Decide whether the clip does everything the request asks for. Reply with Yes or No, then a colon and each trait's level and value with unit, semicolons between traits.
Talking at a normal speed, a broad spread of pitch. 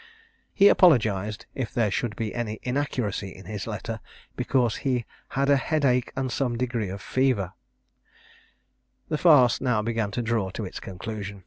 No: average, 160 wpm; average, 3.8 semitones